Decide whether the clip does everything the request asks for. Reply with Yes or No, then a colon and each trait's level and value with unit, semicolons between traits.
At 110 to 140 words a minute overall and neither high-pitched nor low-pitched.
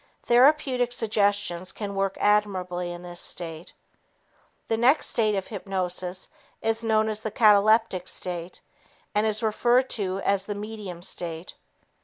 No: slow, 135 wpm; high, 205 Hz